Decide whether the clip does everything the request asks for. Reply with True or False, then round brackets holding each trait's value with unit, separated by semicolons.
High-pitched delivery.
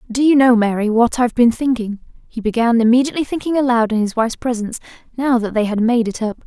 True (235 Hz)